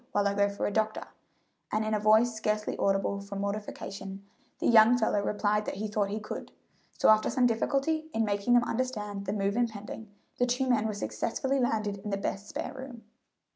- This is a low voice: No, high, 215 Hz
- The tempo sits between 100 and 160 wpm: No, average, 200 wpm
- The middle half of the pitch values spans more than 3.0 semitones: No, average, 2.7 semitones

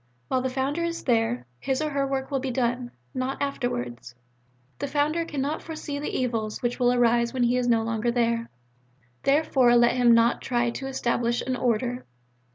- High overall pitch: Yes, very high, 250 Hz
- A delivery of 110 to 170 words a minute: No, average, 180 wpm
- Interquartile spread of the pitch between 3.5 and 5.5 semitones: No, narrow, 2.5 semitones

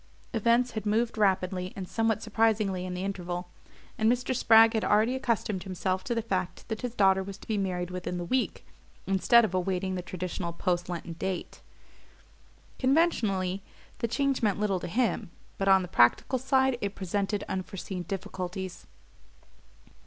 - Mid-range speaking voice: No, high, 195 Hz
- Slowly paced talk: No, average, 160 wpm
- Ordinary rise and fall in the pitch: Yes, average, 3.6 semitones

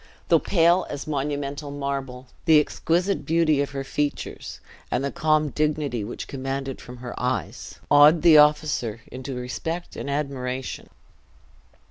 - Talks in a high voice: No, medium, 140 Hz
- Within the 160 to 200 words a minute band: No, slow, 135 wpm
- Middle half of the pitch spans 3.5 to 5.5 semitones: No, average, 2.7 semitones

